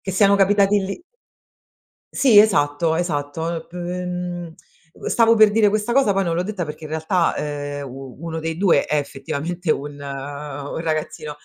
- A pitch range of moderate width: Yes, average, 4.9 semitones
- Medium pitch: Yes, medium, 165 Hz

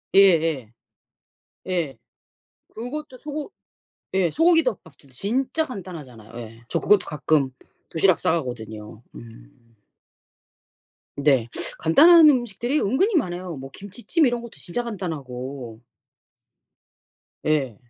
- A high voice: No, medium, 170 Hz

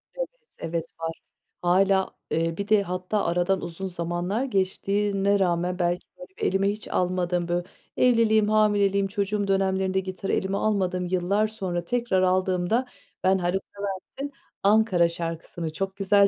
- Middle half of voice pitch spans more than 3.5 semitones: No, narrow, 2.4 semitones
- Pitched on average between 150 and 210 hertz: Yes, high, 190 Hz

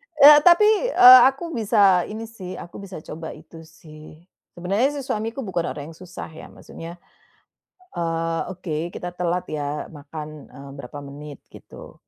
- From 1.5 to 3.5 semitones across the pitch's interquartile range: No, wide, 5.6 semitones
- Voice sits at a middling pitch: Yes, medium, 175 Hz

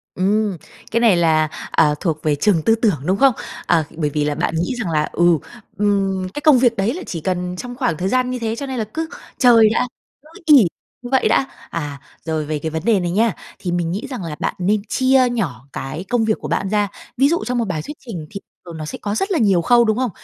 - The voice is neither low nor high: No, high, 200 Hz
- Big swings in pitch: Yes, wide, 6.6 semitones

